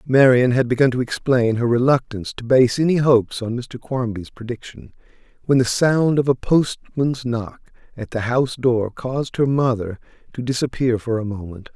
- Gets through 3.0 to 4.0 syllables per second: No, 5.0 syllables/s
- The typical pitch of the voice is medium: No, low, 125 Hz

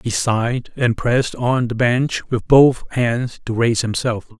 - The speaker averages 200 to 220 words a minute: No, average, 180 wpm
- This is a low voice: Yes, low, 120 Hz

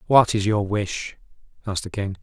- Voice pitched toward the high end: No, low, 105 Hz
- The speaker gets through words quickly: No, average, 190 wpm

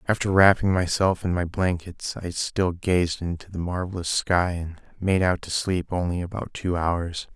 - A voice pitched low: Yes, very low, 90 Hz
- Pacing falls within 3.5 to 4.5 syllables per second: Yes, 4.4 syllables/s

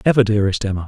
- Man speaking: Yes, male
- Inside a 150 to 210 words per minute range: Yes, fast, 205 wpm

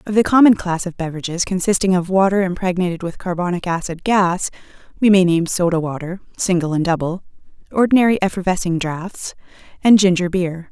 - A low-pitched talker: No, medium, 180 Hz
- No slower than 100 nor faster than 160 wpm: Yes, average, 155 wpm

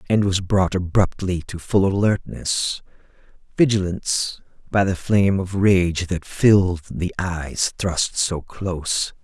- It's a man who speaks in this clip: Yes, male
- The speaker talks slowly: Yes, slow, 130 wpm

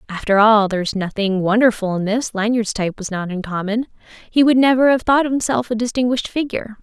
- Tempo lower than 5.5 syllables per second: No, 6.2 syllables/s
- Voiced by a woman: Yes, female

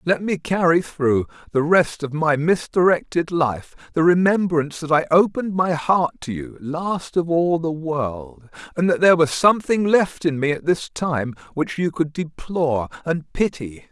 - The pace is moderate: Yes, average, 175 wpm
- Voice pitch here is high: No, medium, 160 Hz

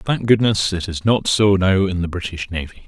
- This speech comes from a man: Yes, male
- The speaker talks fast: Yes, fast, 230 wpm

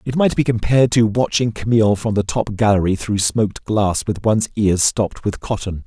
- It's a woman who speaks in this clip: No, male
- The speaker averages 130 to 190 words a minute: No, fast, 205 wpm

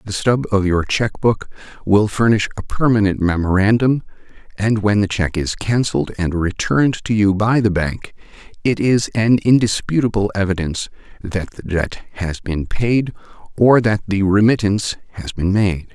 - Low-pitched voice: Yes, low, 105 Hz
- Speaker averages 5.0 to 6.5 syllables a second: No, 4.7 syllables/s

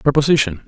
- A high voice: No, low, 130 Hz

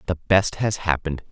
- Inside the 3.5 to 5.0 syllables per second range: No, 5.5 syllables/s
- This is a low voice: Yes, very low, 90 Hz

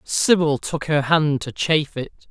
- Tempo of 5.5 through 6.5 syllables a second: No, 4.4 syllables/s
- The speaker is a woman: No, male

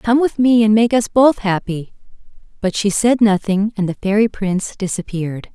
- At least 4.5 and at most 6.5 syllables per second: Yes, 5.0 syllables/s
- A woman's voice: Yes, female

